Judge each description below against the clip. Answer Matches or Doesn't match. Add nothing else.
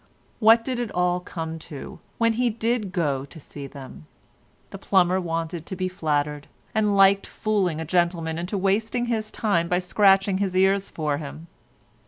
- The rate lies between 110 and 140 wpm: Doesn't match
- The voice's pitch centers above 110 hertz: Matches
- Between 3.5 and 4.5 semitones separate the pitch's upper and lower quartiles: Matches